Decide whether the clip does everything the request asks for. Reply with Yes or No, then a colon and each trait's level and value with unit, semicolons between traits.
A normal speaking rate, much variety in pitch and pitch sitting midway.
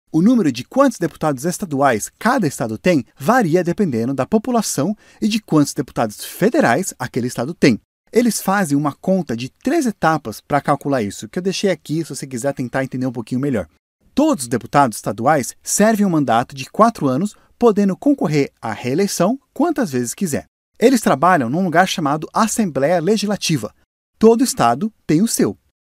Yes: average, 165 wpm; wide, 8.2 semitones; medium, 175 Hz